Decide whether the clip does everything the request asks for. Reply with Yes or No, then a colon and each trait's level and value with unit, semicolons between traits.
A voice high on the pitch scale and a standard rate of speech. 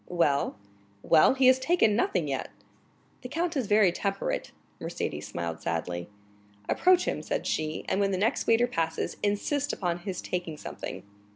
Yes: high, 195 Hz; average, 160 wpm